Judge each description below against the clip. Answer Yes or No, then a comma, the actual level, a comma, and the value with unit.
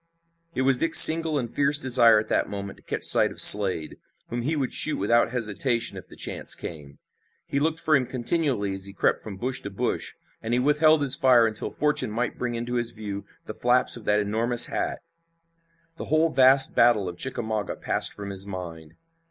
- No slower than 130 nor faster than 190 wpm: No, average, 200 wpm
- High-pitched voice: No, low, 120 Hz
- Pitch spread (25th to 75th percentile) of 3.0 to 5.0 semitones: Yes, average, 4.6 semitones